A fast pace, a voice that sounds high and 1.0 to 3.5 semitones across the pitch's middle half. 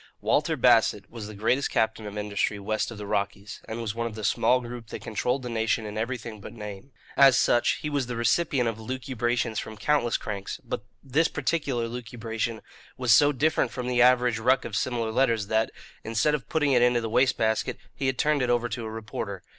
No: fast, 210 wpm; low, 115 Hz; narrow, 2.5 semitones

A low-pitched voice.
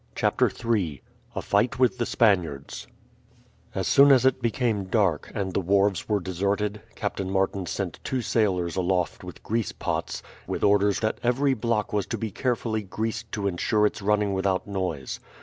Yes: low, 105 Hz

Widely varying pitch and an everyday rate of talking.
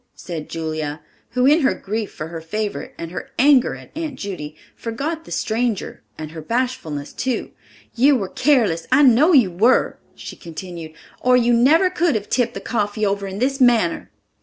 Yes: wide, 7.2 semitones; average, 180 wpm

